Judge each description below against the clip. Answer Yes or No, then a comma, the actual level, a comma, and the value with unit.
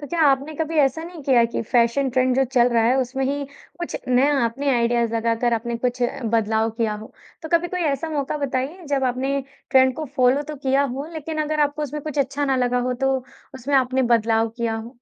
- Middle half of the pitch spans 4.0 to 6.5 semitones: No, average, 3.3 semitones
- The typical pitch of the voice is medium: No, very high, 265 Hz